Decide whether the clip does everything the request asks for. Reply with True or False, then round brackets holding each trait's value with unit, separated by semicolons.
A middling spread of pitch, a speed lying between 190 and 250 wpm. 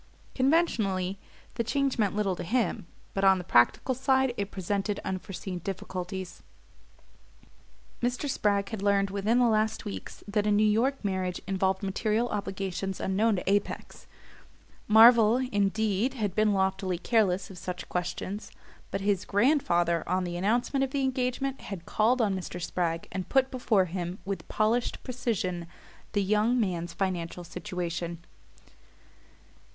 False (3.6 semitones; 145 wpm)